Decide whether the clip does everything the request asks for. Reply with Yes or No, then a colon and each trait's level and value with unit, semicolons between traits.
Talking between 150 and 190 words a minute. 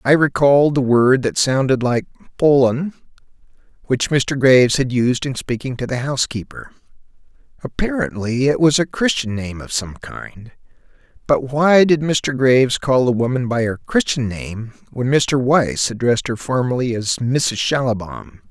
Yes: average, 155 wpm